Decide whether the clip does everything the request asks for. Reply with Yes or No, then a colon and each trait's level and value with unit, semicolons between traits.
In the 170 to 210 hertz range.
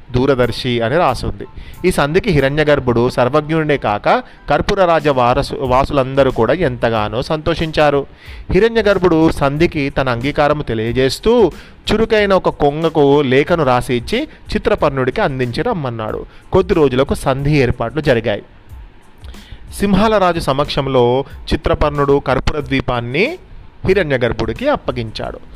No: medium, 145 Hz